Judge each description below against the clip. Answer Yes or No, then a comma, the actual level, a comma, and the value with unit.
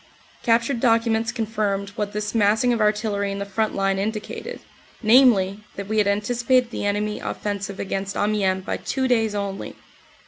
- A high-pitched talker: Yes, high, 210 Hz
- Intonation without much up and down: Yes, narrow, 2.3 semitones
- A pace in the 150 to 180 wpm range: Yes, average, 160 wpm